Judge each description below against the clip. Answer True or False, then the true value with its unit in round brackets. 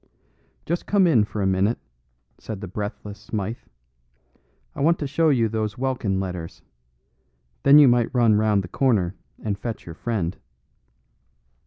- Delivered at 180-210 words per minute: False (150 wpm)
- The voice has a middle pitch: False (110 Hz)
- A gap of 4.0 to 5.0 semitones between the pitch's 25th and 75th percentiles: True (4.7 semitones)